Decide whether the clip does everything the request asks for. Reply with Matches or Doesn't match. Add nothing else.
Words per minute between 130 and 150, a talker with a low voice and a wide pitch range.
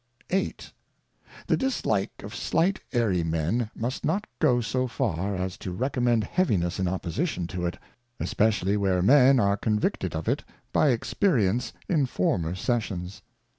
Matches